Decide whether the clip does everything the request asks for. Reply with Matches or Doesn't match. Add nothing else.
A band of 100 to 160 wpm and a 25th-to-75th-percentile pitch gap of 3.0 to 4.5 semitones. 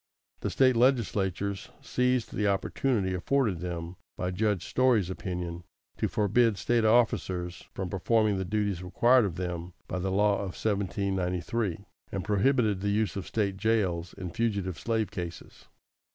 Matches